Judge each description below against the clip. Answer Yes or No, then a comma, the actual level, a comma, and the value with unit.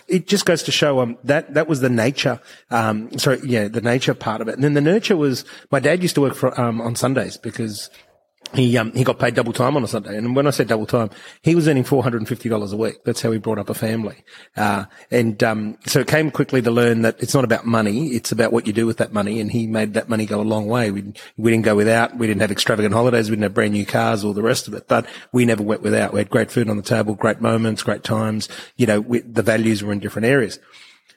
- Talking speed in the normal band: No, fast, 275 wpm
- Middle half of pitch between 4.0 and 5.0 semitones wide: No, average, 2.8 semitones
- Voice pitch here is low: Yes, low, 115 Hz